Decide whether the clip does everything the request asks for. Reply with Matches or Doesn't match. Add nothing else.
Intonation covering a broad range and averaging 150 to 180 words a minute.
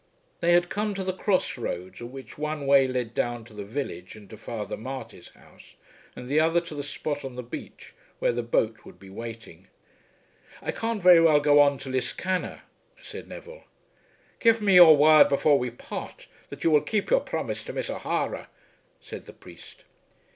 Doesn't match